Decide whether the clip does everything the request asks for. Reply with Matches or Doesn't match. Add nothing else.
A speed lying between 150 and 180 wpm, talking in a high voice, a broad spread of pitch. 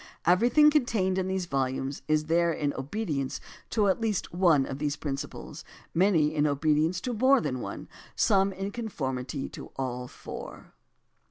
Doesn't match